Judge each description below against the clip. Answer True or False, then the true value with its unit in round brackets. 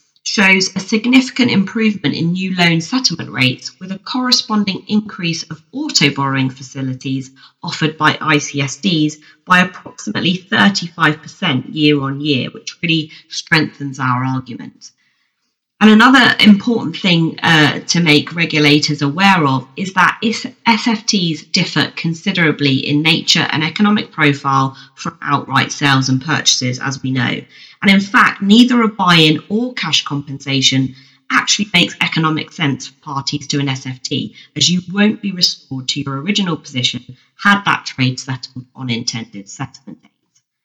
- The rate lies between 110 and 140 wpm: True (135 wpm)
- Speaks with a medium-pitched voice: True (155 Hz)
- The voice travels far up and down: True (6.0 semitones)